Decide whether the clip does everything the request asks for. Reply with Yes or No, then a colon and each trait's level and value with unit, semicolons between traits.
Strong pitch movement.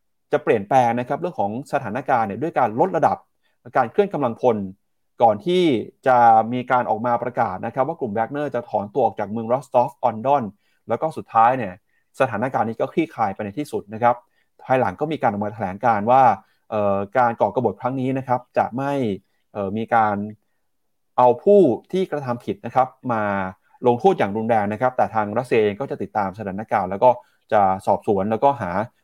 No: average, 4.0 semitones